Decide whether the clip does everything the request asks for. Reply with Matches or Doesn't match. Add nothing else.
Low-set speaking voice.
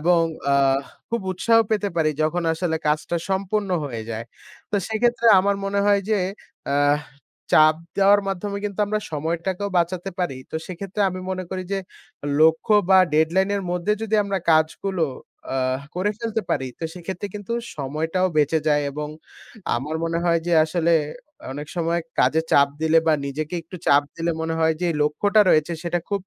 Doesn't match